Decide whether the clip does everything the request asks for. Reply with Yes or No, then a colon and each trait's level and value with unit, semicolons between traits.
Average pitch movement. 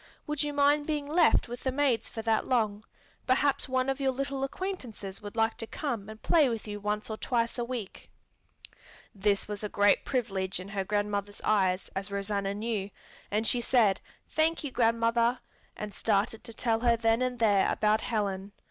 Yes: average, 3.9 semitones